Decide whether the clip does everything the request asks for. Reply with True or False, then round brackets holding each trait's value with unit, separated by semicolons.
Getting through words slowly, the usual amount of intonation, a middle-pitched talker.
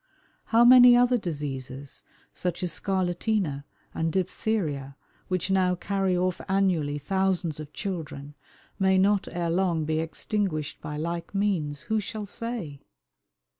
True (130 wpm; 4.4 semitones; 180 Hz)